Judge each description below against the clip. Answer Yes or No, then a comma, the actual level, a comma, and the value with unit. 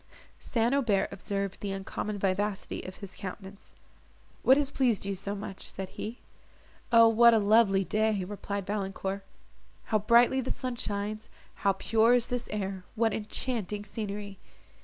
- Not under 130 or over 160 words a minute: Yes, average, 150 wpm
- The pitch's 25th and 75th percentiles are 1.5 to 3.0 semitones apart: Yes, average, 2.7 semitones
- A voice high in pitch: Yes, high, 210 Hz